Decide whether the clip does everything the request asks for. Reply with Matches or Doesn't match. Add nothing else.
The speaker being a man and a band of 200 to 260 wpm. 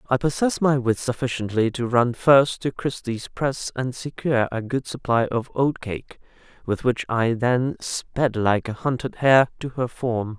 Doesn't match